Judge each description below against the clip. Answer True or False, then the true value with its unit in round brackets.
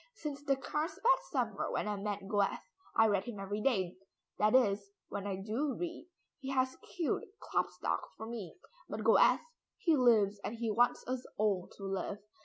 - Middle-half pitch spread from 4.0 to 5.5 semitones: True (5.1 semitones)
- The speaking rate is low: False (175 wpm)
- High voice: True (220 Hz)